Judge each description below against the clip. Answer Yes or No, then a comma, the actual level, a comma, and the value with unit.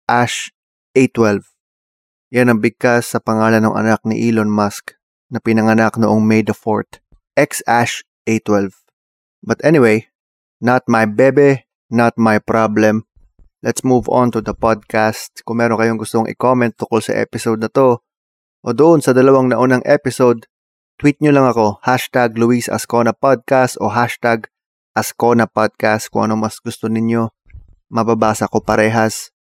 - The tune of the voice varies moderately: No, narrow, 1.9 semitones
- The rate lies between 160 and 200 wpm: No, average, 145 wpm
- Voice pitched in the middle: No, low, 115 Hz